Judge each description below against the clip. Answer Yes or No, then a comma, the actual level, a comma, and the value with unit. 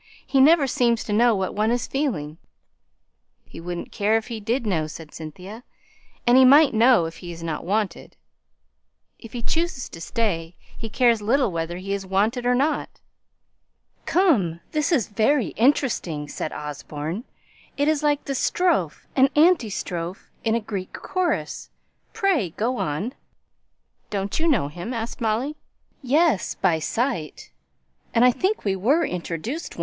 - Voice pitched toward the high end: Yes, high, 225 Hz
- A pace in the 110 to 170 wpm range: Yes, average, 155 wpm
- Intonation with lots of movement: Yes, wide, 7.1 semitones